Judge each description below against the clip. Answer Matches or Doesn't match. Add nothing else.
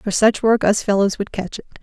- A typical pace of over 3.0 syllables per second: Matches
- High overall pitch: Matches